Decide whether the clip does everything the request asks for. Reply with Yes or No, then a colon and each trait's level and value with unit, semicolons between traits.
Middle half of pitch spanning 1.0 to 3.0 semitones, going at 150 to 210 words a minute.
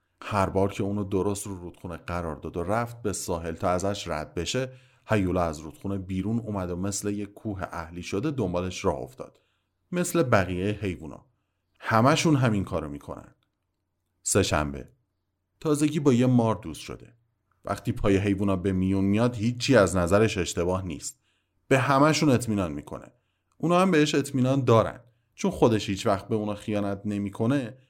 No: average, 4.3 semitones; fast, 155 wpm